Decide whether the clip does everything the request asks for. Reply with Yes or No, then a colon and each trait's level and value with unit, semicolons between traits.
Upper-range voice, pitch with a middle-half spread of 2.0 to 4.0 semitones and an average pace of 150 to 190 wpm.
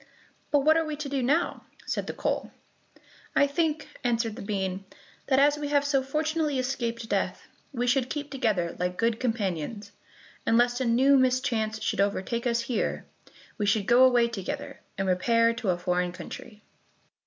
No: high, 240 Hz; average, 4.8 semitones; average, 175 wpm